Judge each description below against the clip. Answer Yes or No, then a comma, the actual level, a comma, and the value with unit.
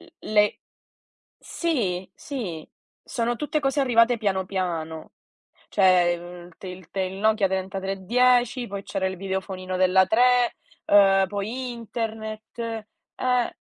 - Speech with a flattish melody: No, average, 4.1 semitones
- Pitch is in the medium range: No, high, 200 Hz